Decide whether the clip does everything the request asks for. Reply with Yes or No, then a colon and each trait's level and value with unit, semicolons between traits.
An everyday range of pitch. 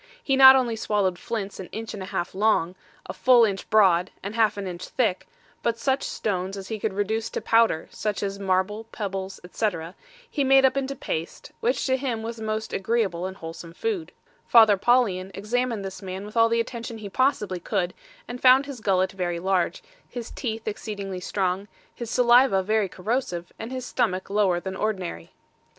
Yes: average, 3.8 semitones